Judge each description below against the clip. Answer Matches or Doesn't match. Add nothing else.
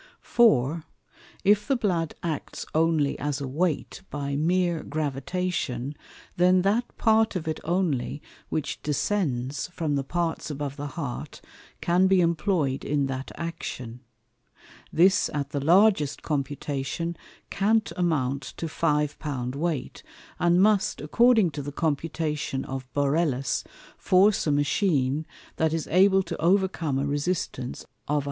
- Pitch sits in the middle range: Matches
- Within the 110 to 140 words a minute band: Matches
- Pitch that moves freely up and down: Doesn't match